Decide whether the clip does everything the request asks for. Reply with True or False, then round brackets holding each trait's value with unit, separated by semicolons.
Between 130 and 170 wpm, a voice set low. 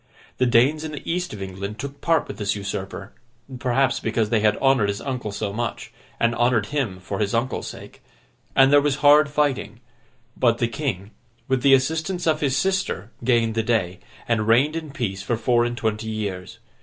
False (195 wpm; 120 Hz)